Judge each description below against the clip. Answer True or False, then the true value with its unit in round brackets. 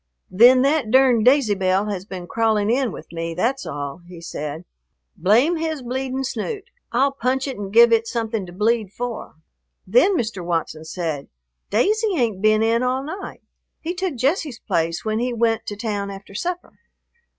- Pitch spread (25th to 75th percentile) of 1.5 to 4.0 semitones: False (5.4 semitones)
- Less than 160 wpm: False (175 wpm)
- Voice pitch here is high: True (230 Hz)